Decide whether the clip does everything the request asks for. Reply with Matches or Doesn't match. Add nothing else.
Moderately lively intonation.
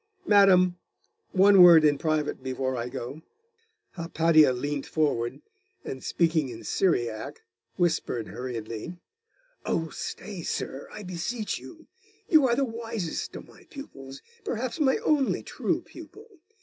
Doesn't match